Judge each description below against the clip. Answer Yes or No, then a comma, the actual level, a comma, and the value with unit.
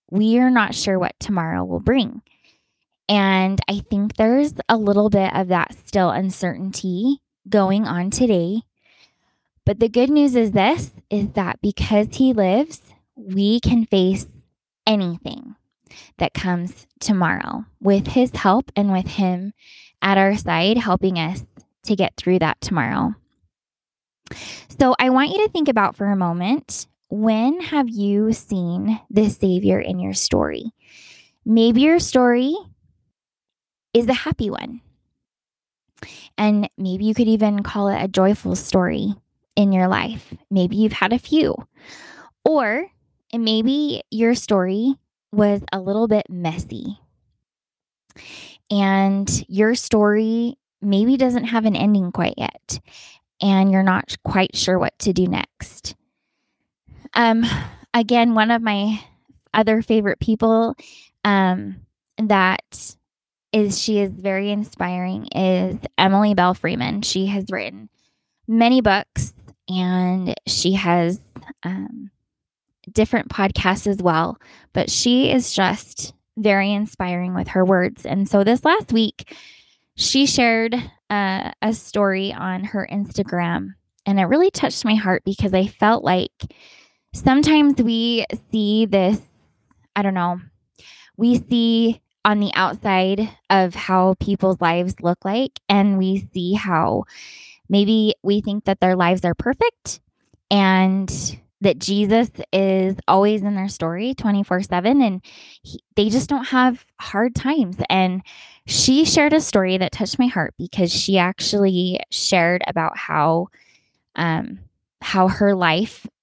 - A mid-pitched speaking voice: No, high, 205 Hz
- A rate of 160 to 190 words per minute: No, slow, 135 wpm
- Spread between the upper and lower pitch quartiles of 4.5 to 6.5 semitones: No, average, 3.5 semitones